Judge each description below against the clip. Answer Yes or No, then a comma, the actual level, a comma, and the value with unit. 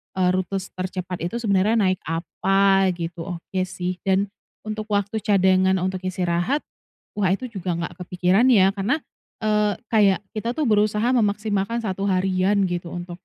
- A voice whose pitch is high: Yes, high, 195 Hz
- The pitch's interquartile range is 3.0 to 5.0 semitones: No, narrow, 2.4 semitones